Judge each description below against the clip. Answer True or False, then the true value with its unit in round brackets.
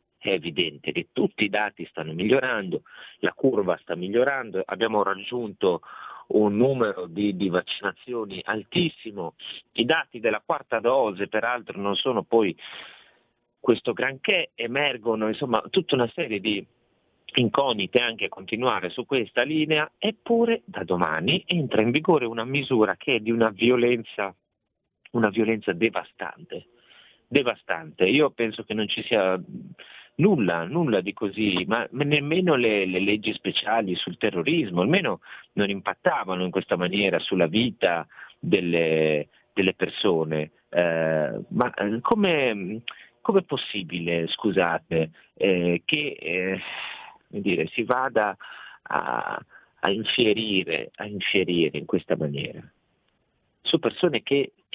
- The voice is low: True (105 Hz)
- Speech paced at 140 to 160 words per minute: False (125 wpm)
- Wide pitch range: False (4.6 semitones)